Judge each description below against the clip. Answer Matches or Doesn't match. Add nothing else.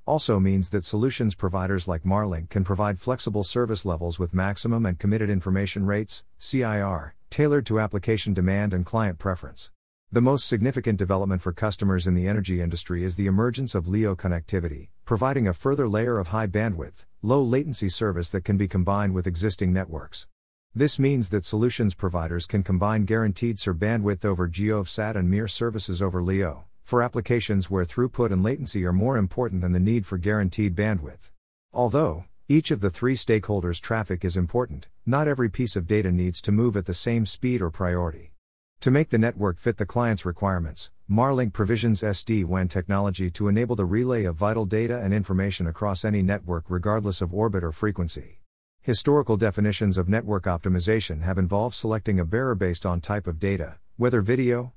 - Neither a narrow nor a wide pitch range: Matches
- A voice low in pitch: Matches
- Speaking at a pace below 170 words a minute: Doesn't match